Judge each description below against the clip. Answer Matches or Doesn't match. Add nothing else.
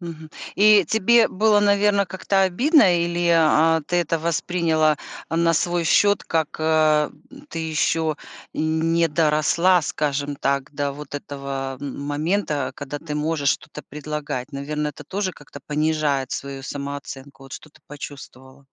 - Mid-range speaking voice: Matches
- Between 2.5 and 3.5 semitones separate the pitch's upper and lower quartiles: Matches